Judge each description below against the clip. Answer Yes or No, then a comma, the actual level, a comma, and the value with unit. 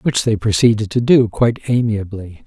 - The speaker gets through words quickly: No, average, 170 wpm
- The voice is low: Yes, low, 110 Hz